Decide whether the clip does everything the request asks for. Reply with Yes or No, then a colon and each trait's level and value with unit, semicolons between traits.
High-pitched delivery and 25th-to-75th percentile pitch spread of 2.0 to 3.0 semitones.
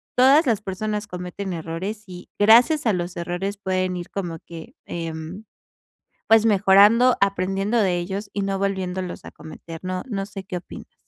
Yes: high, 195 Hz; average, 2.7 semitones